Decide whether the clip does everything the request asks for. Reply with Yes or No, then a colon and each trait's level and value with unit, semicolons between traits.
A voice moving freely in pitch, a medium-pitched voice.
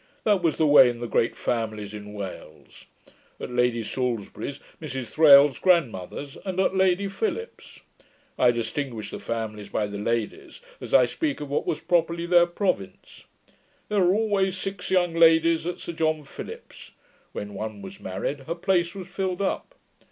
Yes: wide, 7.9 semitones; medium, 155 Hz